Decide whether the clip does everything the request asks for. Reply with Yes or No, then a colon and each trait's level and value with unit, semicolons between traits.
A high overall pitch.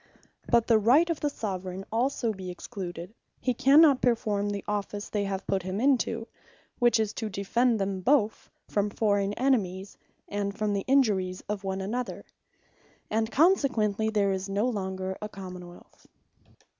Yes: high, 205 Hz